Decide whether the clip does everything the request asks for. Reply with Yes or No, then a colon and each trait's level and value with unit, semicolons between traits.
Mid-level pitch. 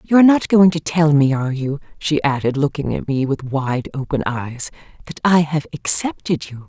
Yes: medium, 150 Hz